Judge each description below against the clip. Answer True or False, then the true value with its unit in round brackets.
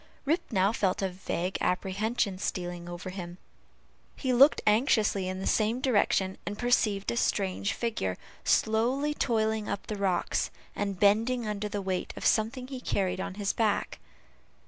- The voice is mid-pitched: False (205 Hz)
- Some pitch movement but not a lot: True (3.5 semitones)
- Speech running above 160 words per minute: False (155 wpm)